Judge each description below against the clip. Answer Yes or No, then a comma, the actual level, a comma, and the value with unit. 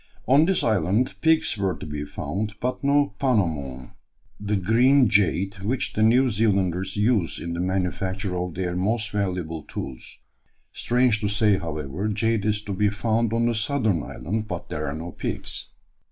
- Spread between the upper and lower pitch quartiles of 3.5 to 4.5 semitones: Yes, average, 4.1 semitones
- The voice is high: No, low, 100 Hz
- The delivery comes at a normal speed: Yes, average, 170 wpm